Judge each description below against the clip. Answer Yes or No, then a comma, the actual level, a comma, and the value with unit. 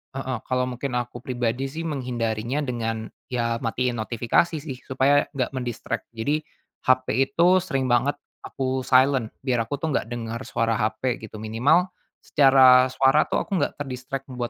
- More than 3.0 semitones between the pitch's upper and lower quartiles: No, narrow, 2.5 semitones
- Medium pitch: No, low, 130 Hz